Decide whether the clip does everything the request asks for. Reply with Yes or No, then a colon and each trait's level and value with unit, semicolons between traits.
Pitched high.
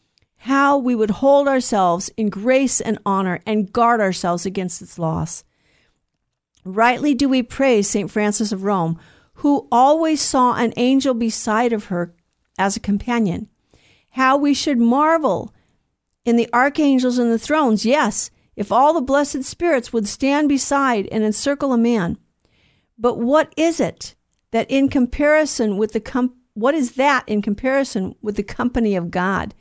Yes: high, 235 Hz